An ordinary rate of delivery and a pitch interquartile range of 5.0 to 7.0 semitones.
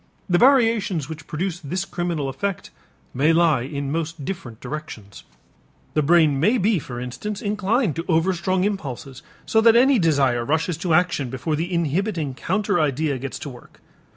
Yes: average, 160 wpm; average, 5.3 semitones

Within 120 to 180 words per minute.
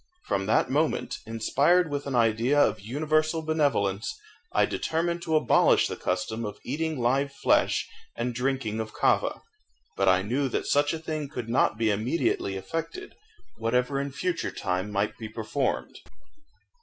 Yes: average, 155 wpm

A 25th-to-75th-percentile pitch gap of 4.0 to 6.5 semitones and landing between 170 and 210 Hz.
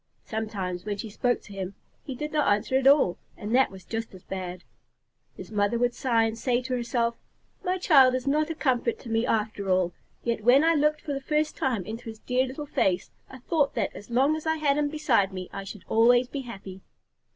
No: average, 5.1 semitones; high, 240 Hz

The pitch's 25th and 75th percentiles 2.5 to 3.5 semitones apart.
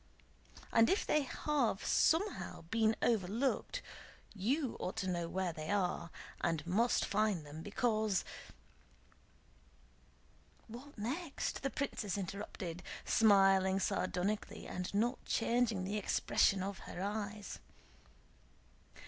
No: average, 3.9 semitones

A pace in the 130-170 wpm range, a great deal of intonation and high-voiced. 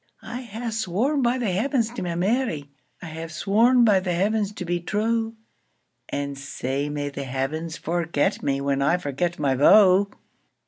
No: average, 150 wpm; wide, 7.5 semitones; medium, 180 Hz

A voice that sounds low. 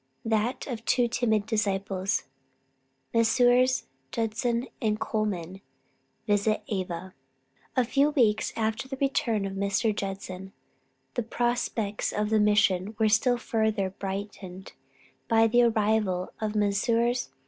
No: high, 215 Hz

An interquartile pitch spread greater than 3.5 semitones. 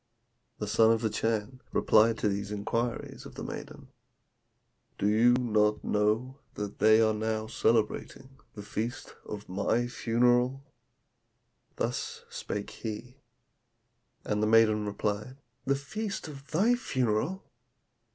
No: average, 3.0 semitones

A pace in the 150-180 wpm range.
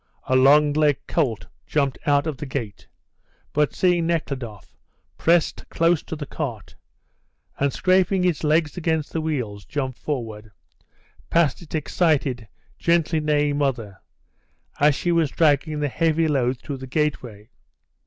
No: average, 140 wpm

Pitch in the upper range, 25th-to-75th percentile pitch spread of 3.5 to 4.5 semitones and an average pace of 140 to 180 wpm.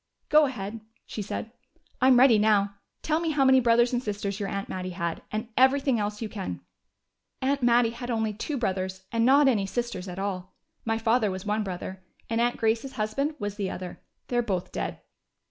No: high, 225 Hz; average, 3.8 semitones; average, 195 wpm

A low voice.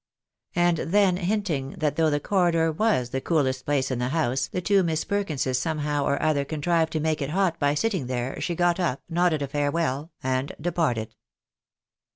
No: medium, 155 Hz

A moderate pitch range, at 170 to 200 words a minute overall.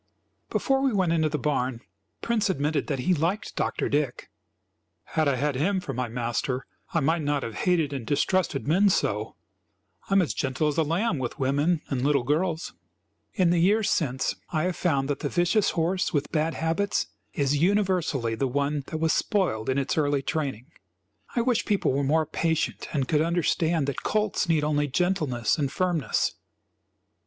Yes: average, 4.4 semitones; average, 180 wpm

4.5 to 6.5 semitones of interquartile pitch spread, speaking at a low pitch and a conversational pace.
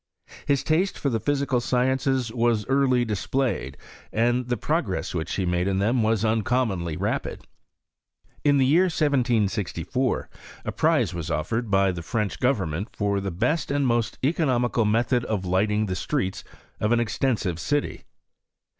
Yes: average, 5.1 semitones; low, 115 Hz; average, 155 wpm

